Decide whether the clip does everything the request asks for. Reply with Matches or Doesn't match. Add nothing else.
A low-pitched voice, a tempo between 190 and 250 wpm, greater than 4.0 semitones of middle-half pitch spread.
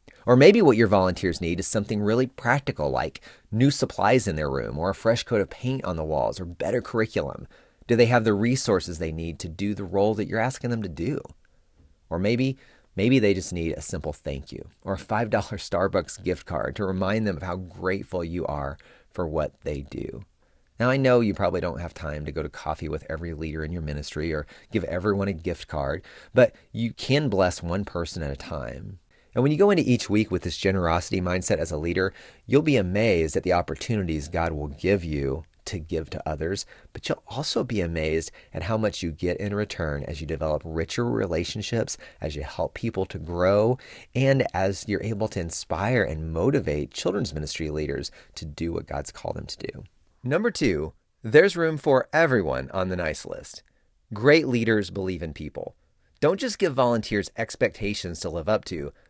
Matches